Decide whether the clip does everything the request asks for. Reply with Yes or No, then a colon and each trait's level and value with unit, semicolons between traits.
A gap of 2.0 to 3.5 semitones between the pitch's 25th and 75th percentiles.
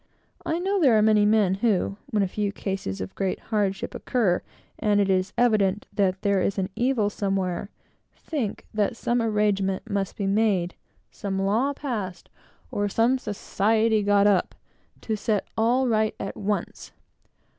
Yes: narrow, 2.4 semitones